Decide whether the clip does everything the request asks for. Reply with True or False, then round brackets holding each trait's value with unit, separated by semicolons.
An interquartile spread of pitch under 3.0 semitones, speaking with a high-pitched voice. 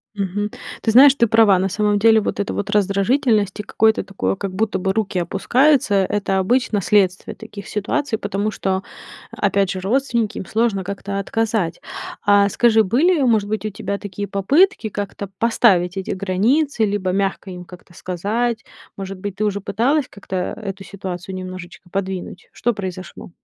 True (2.6 semitones; 200 Hz)